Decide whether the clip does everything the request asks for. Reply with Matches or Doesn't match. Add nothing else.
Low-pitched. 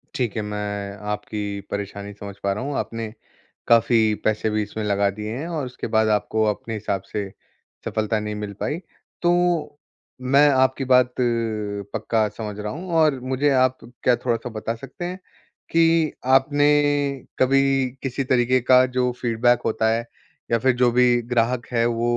Matches